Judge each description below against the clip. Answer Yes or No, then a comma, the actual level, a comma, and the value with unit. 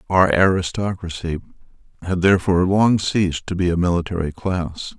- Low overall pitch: Yes, very low, 90 Hz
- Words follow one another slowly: Yes, slow, 130 wpm